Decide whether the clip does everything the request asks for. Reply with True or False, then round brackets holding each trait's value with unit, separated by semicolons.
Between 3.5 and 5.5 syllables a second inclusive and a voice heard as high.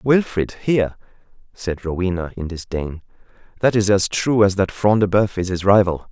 False (5.0 syllables/s; 100 Hz)